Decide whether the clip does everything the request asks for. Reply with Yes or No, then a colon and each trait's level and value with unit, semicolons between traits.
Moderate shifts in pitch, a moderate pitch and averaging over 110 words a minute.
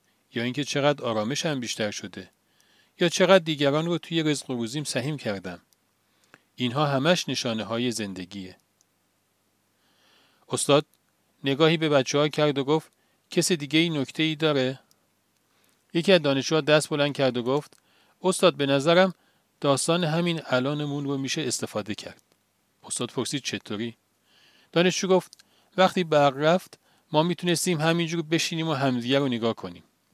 Yes: average, 4.9 semitones; medium, 145 Hz; average, 140 wpm